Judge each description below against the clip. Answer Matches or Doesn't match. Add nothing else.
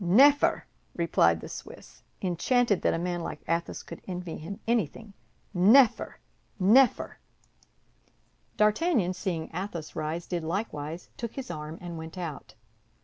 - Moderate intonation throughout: Matches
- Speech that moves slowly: Matches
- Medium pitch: Matches